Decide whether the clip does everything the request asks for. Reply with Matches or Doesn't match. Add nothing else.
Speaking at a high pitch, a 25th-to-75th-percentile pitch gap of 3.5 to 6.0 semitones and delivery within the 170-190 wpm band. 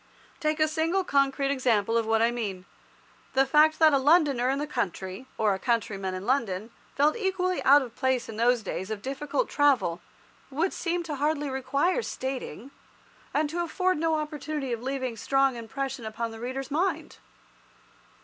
Matches